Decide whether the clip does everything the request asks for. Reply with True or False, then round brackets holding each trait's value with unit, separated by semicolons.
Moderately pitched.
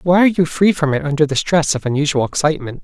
True (155 Hz)